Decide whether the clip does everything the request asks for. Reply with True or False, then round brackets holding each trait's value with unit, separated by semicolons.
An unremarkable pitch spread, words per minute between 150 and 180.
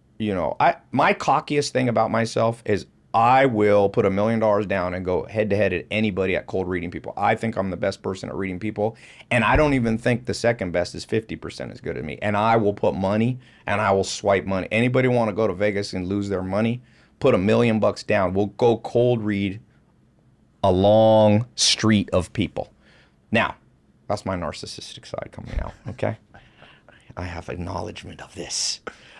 False (3.0 semitones; 200 wpm)